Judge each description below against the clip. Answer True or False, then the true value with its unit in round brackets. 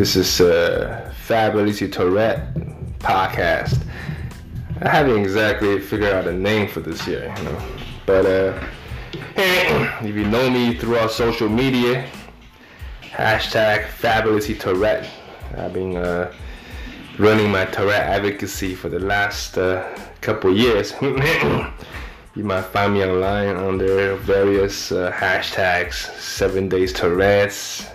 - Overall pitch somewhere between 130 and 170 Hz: False (100 Hz)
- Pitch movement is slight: True (2.3 semitones)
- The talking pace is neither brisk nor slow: False (120 wpm)